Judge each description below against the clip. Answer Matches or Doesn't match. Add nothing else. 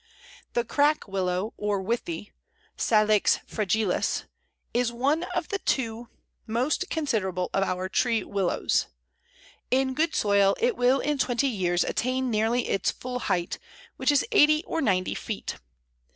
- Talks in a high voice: Matches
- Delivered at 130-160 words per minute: Matches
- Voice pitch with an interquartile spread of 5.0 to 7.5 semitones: Matches